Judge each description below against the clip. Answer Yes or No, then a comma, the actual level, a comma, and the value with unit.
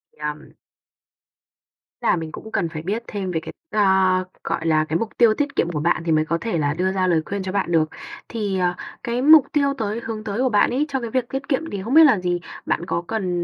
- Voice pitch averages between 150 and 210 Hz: Yes, high, 195 Hz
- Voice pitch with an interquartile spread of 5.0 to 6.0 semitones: Yes, average, 5.3 semitones